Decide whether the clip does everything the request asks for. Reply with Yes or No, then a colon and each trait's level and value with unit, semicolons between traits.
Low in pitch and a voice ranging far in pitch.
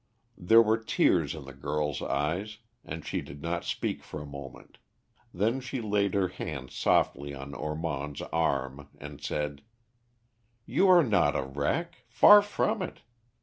Yes: very low, 75 Hz; wide, 7.4 semitones